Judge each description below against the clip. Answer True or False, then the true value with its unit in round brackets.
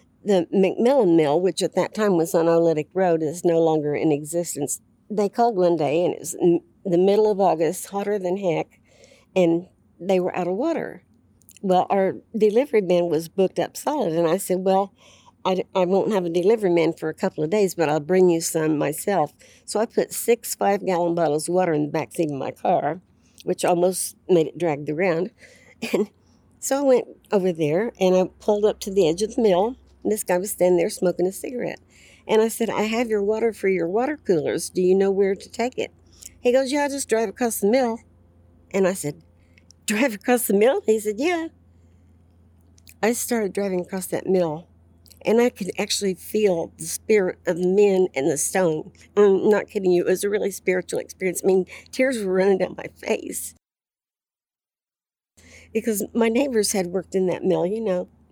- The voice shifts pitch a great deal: False (4.0 semitones)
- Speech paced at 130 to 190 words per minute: False (205 wpm)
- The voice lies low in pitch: False (185 Hz)